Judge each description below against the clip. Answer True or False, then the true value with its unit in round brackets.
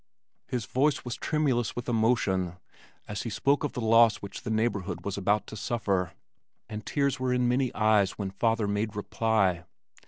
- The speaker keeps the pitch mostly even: False (3.4 semitones)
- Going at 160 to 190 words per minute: True (175 wpm)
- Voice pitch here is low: True (110 Hz)